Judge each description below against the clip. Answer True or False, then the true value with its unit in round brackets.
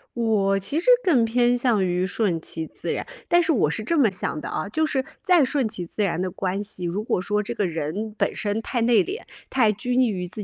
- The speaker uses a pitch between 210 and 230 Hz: True (215 Hz)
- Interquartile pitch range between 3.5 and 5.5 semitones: True (4.9 semitones)